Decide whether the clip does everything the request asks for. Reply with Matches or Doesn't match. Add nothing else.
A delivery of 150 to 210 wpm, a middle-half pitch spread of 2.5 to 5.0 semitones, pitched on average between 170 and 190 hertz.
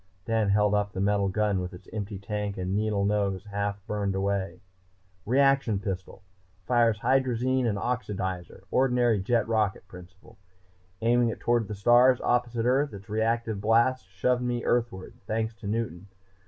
Doesn't match